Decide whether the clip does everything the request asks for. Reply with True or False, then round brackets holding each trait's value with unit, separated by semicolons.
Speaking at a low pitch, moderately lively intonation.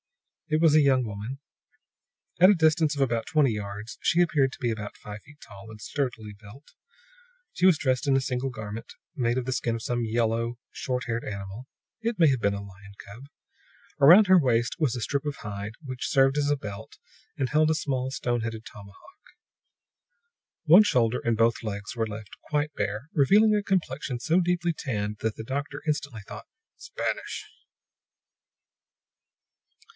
True (125 Hz; 5.0 semitones)